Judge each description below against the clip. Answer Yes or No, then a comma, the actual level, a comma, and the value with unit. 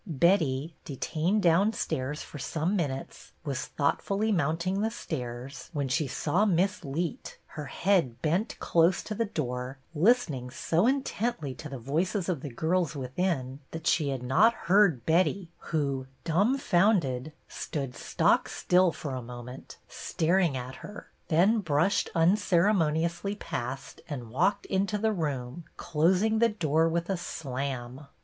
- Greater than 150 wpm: No, average, 140 wpm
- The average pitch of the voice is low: No, medium, 165 Hz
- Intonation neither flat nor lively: No, wide, 5.9 semitones